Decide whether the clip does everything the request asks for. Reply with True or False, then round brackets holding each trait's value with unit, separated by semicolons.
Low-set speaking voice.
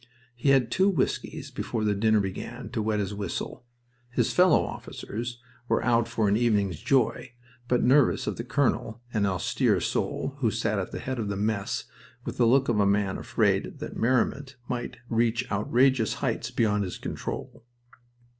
True (115 Hz)